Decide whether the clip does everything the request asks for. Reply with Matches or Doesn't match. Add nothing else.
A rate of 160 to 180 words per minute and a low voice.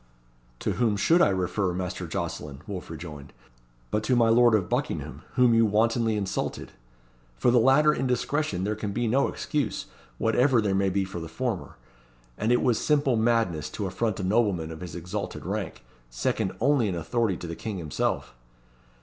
Matches